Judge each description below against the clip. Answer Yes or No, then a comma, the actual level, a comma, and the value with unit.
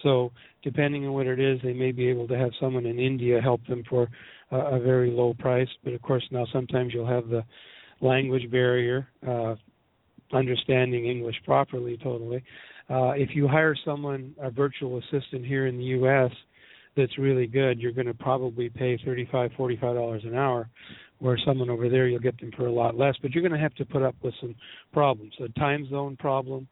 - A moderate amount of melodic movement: No, narrow, 1.7 semitones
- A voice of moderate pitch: No, low, 130 Hz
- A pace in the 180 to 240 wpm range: Yes, average, 200 wpm